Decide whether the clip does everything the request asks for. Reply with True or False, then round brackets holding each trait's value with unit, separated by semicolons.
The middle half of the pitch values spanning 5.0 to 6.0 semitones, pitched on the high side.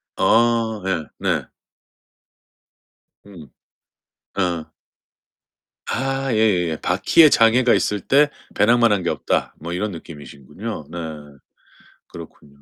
False (5.5 semitones; 105 Hz)